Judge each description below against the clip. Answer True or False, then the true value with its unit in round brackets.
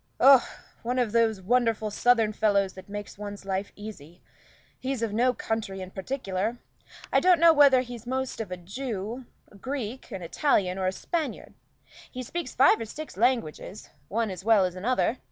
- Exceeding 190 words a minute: False (175 wpm)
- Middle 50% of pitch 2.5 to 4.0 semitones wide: False (4.6 semitones)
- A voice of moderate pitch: False (225 Hz)